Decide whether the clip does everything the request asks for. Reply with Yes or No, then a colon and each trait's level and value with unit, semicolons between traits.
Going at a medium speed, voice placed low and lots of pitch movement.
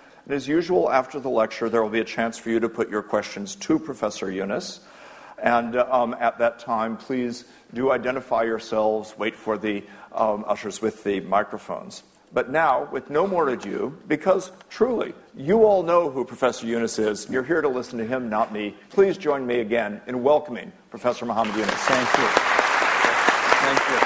No: average, 180 wpm; low, 120 Hz; average, 3.8 semitones